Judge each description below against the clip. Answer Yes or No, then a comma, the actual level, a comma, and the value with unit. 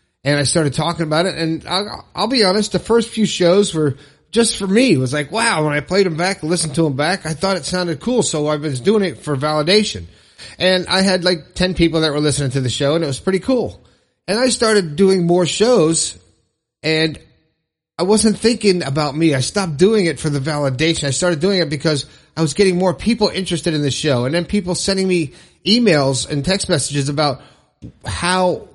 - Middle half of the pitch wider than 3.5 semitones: Yes, average, 4.4 semitones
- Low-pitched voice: No, medium, 165 Hz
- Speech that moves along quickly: Yes, fast, 220 wpm